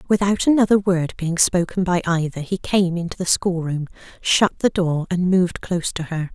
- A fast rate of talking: No, average, 190 wpm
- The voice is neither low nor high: Yes, medium, 180 Hz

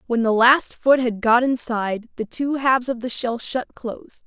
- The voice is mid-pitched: No, high, 245 Hz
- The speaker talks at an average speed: No, fast, 210 wpm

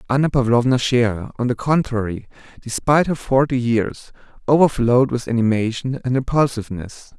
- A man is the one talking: Yes, male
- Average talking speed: No, slow, 125 wpm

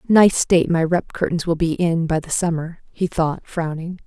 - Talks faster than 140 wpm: Yes, fast, 205 wpm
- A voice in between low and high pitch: Yes, medium, 170 Hz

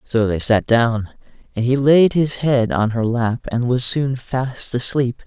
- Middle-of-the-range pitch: No, low, 125 Hz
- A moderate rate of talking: Yes, average, 195 wpm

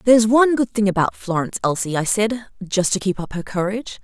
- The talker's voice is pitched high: Yes, high, 205 Hz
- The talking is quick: Yes, fast, 225 wpm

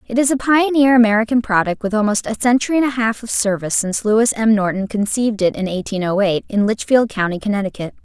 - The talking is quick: Yes, fast, 215 wpm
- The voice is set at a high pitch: Yes, high, 220 Hz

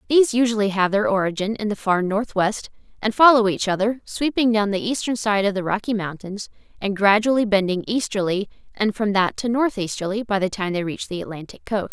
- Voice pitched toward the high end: Yes, high, 205 Hz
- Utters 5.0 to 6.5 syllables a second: Yes, 5.7 syllables/s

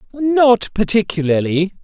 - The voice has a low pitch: No, high, 210 Hz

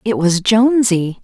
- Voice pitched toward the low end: No, high, 205 Hz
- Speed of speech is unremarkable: Yes, average, 145 wpm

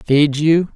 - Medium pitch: Yes, medium, 150 Hz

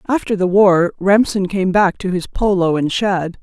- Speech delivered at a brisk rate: No, average, 195 wpm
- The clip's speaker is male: No, female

